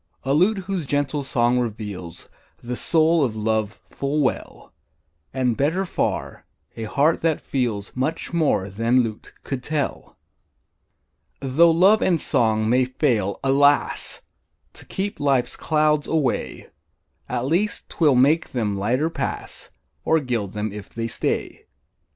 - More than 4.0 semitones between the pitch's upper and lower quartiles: Yes, average, 5.3 semitones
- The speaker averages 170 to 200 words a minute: No, slow, 135 wpm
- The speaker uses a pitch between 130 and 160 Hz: Yes, low, 135 Hz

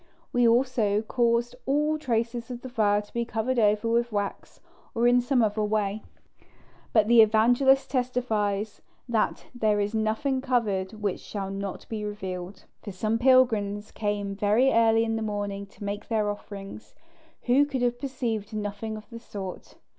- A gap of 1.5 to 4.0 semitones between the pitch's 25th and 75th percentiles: Yes, average, 2.9 semitones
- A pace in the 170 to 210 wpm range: No, average, 160 wpm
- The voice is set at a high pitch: Yes, high, 220 Hz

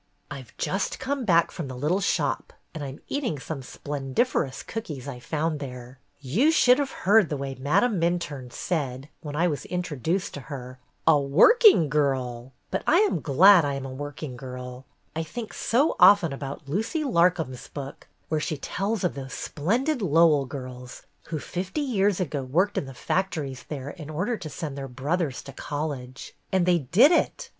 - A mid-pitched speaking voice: Yes, medium, 155 Hz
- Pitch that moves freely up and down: Yes, wide, 5.8 semitones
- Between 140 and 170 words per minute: No, average, 185 wpm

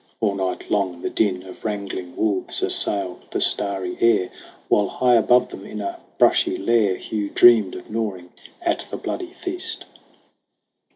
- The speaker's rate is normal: Yes, average, 155 wpm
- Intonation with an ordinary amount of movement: Yes, average, 3.4 semitones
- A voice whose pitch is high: No, low, 100 Hz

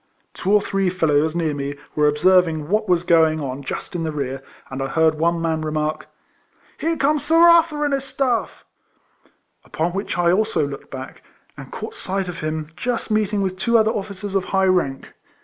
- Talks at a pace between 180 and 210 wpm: Yes, average, 200 wpm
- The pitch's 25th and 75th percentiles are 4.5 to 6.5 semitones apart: Yes, average, 5.3 semitones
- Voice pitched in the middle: Yes, medium, 175 Hz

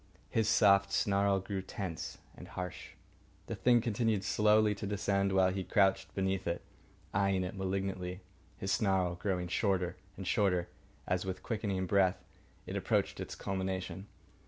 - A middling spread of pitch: No, narrow, 1.4 semitones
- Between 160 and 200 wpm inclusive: No, average, 145 wpm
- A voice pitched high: No, very low, 95 Hz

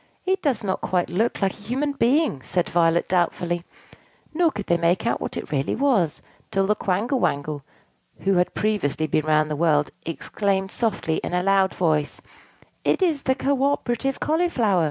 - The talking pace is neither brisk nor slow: Yes, average, 175 wpm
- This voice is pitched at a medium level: No, high, 195 Hz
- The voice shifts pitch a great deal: Yes, wide, 7.1 semitones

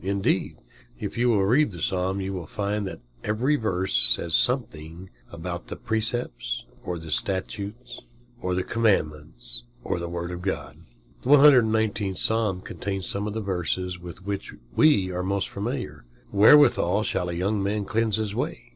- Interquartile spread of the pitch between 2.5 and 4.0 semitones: Yes, average, 3.7 semitones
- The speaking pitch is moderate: No, low, 100 Hz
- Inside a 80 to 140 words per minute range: No, average, 165 wpm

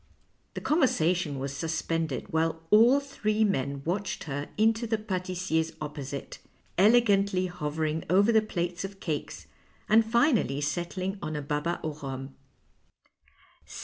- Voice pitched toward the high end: No, medium, 175 Hz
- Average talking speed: No, slow, 125 wpm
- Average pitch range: No, wide, 5.9 semitones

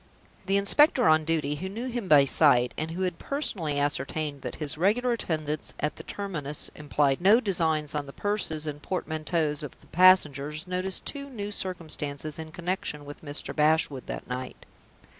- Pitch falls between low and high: Yes, medium, 155 Hz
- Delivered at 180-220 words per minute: No, average, 170 wpm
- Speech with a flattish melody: No, average, 4.3 semitones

